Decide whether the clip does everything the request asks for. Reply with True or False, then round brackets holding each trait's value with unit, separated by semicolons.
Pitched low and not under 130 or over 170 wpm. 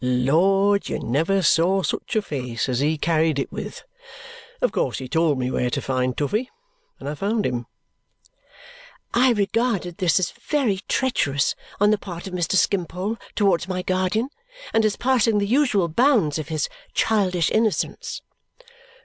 False (185 Hz; 160 wpm)